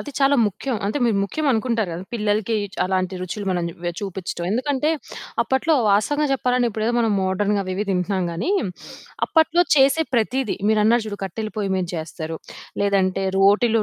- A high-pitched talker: Yes, high, 210 Hz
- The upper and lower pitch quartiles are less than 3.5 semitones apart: No, average, 4.7 semitones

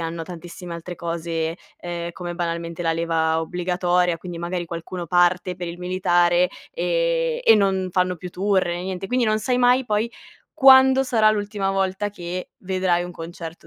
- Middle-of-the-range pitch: Yes, medium, 180 Hz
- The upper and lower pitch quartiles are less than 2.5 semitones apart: No, average, 2.8 semitones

